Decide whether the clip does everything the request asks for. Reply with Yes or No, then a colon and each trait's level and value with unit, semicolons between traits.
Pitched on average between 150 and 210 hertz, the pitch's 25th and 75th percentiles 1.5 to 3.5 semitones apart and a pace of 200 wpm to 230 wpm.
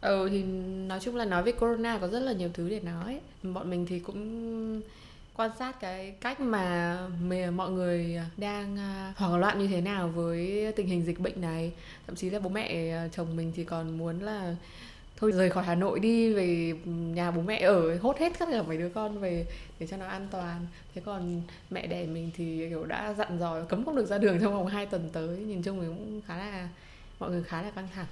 Yes: medium, 185 Hz; average, 3.2 semitones; average, 225 wpm